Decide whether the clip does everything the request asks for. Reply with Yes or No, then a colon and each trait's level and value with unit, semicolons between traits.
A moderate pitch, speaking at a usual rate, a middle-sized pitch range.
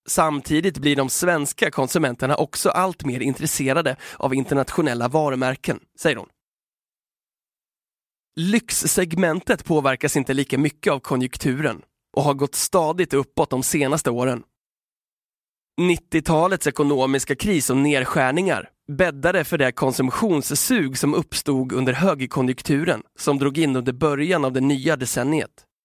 No: medium, 145 Hz; slow, 120 wpm; average, 3.5 semitones